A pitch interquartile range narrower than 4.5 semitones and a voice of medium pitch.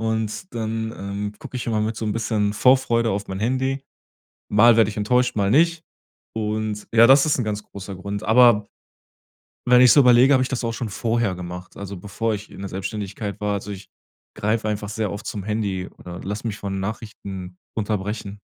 No: narrow, 2.5 semitones; low, 105 Hz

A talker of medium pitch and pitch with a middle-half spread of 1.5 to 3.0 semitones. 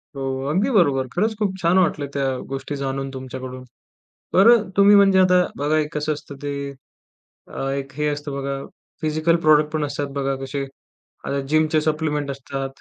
Yes: medium, 150 Hz; average, 2.7 semitones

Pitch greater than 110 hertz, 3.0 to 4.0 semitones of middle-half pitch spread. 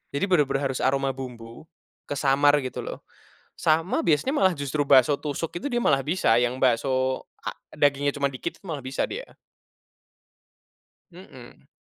Yes: medium, 140 Hz; average, 3.4 semitones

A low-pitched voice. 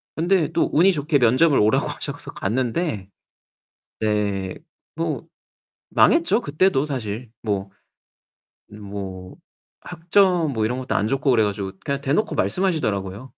Yes: low, 130 Hz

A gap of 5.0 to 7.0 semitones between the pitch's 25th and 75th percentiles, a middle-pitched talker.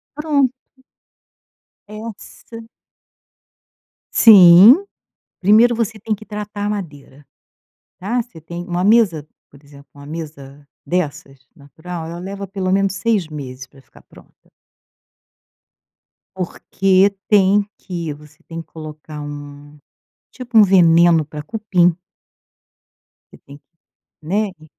Yes: wide, 5.6 semitones; medium, 180 Hz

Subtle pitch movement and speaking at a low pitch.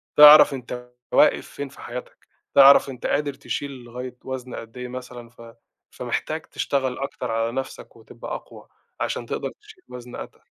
Yes: narrow, 2.1 semitones; low, 125 Hz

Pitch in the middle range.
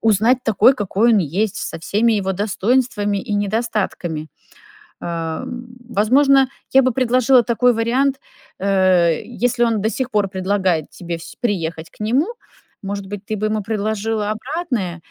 No: high, 215 Hz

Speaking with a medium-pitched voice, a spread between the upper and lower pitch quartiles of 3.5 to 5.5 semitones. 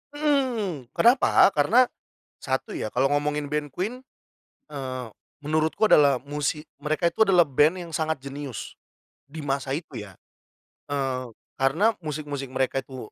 Yes: medium, 145 Hz; average, 4.0 semitones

